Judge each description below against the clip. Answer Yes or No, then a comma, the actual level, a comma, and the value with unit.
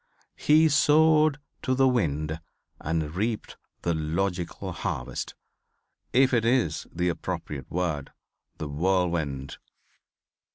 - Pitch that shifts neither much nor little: No, wide, 8.6 semitones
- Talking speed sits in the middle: No, slow, 100 wpm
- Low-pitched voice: Yes, very low, 90 Hz